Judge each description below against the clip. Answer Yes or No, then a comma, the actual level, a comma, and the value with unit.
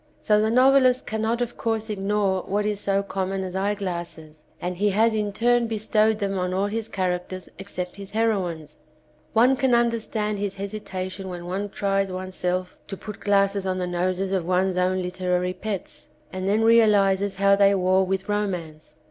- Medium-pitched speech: No, high, 195 Hz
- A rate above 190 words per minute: No, average, 175 wpm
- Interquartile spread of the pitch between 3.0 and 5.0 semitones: No, narrow, 2.4 semitones